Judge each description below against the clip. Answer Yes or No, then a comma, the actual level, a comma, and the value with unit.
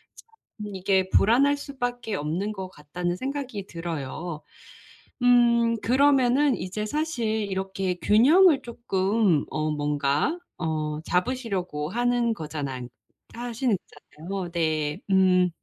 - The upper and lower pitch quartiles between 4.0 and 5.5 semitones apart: No, wide, 6.2 semitones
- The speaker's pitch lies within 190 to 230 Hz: Yes, high, 200 Hz